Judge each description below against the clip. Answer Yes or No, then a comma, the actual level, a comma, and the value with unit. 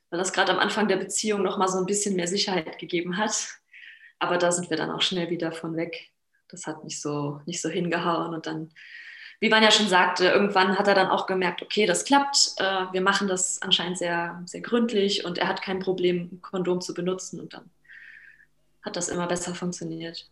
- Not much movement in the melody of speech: Yes, narrow, 2.2 semitones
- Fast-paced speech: Yes, fast, 215 wpm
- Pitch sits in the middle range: Yes, medium, 180 Hz